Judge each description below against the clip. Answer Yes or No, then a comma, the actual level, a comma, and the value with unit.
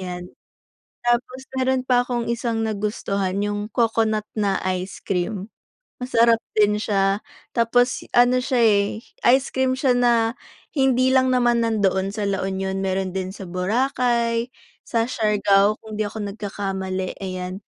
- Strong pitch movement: No, average, 3.8 semitones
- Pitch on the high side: Yes, high, 215 Hz